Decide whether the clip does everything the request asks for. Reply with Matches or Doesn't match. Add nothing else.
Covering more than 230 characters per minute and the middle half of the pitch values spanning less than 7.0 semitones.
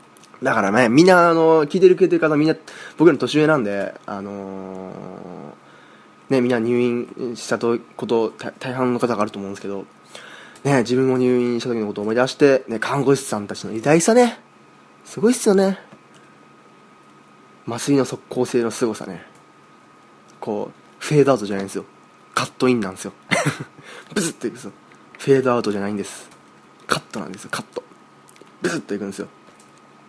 Matches